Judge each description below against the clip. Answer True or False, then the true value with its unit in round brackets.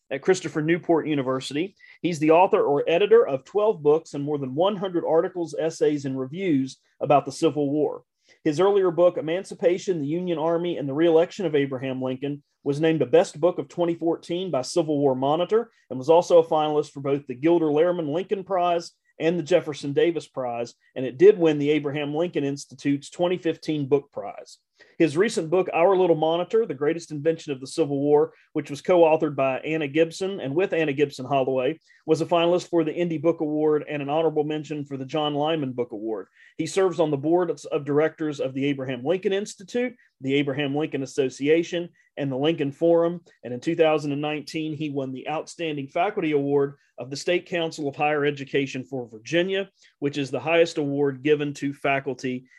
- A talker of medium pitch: True (155 Hz)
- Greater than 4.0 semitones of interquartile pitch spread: False (3.1 semitones)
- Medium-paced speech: True (185 wpm)